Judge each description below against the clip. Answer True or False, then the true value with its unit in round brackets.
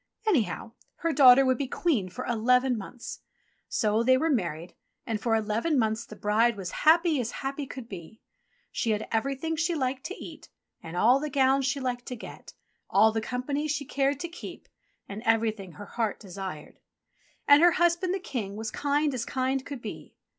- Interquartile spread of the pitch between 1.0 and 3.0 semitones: False (4.6 semitones)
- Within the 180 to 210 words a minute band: True (185 wpm)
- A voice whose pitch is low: False (250 Hz)